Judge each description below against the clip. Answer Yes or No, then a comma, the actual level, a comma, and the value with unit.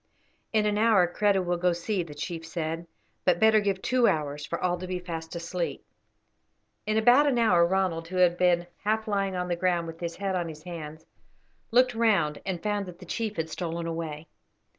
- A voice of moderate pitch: Yes, medium, 180 Hz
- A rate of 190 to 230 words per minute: Yes, fast, 205 wpm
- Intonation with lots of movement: No, average, 3.6 semitones